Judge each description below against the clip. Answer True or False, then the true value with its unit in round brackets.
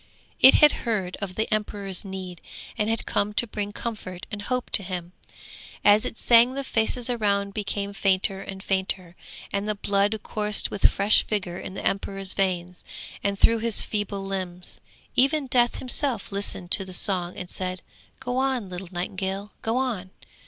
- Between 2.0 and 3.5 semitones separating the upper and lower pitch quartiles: True (2.8 semitones)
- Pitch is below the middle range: False (200 Hz)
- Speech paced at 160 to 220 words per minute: True (170 wpm)